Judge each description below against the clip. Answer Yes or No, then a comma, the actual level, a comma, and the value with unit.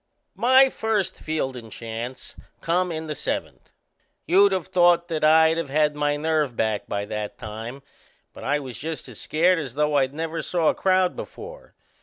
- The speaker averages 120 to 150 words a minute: No, average, 175 wpm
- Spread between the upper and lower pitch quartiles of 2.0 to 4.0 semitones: No, average, 4.8 semitones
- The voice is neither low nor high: Yes, medium, 155 Hz